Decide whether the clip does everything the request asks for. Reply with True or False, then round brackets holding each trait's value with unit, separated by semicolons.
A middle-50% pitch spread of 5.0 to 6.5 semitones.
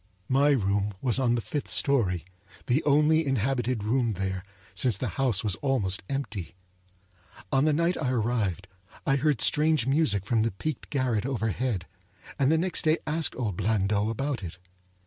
True (5.3 semitones)